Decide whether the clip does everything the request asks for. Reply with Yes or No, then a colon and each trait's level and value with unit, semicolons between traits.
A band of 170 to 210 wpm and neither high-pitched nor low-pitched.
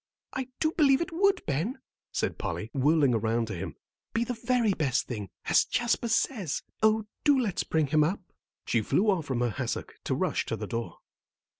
Yes: average, 190 wpm; medium, 180 Hz